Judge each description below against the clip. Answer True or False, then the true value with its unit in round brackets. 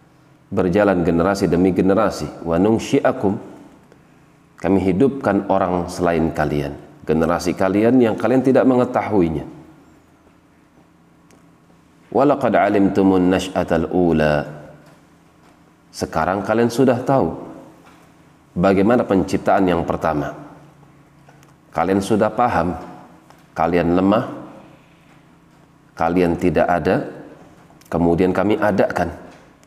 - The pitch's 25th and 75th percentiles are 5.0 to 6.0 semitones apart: True (5.5 semitones)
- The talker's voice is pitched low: True (95 Hz)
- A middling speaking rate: False (70 wpm)